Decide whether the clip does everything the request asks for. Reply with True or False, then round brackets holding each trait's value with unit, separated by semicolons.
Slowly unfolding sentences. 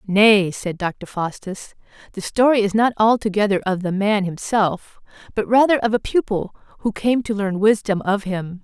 False (175 wpm)